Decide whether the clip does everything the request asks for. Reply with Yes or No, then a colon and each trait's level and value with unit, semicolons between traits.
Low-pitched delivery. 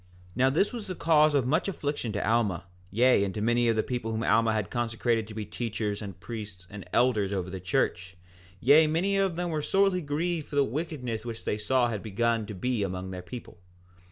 Yes: low, 115 Hz